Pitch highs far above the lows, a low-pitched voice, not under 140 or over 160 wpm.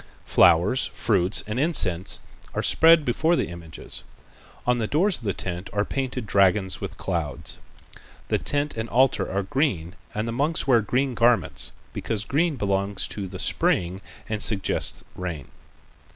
Yes: wide, 6.0 semitones; low, 105 Hz; average, 150 wpm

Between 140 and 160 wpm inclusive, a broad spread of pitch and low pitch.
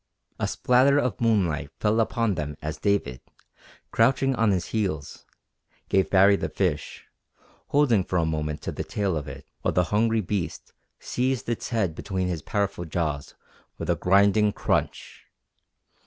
Yes: average, 155 wpm; wide, 5.8 semitones; very low, 95 Hz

